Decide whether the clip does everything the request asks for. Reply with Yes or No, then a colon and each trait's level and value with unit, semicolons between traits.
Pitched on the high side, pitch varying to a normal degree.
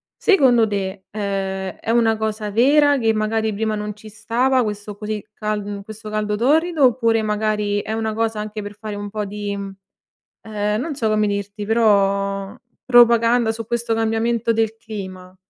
No: high, 215 Hz; narrow, 1.8 semitones